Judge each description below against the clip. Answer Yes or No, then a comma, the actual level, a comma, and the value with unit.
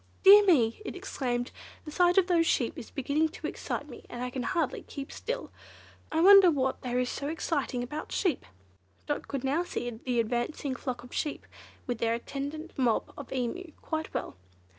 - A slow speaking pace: No, average, 185 wpm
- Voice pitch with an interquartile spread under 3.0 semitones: No, average, 5.0 semitones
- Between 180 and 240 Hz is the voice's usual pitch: No, very high, 280 Hz